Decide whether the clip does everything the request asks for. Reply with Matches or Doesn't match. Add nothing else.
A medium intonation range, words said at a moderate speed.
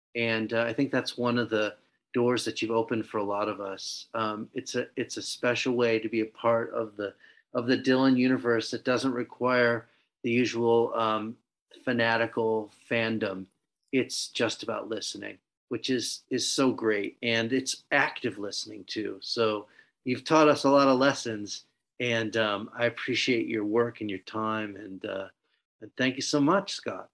Doesn't match